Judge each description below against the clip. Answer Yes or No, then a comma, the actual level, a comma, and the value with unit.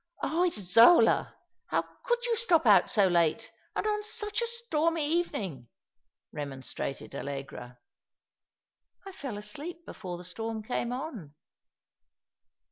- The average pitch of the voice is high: Yes, high, 240 Hz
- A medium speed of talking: No, slow, 130 wpm